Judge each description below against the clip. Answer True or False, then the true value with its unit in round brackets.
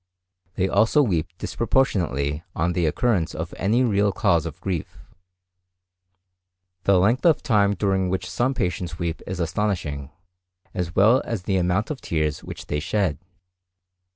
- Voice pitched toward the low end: True (95 Hz)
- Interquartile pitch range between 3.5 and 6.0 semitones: True (4.3 semitones)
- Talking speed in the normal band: True (145 wpm)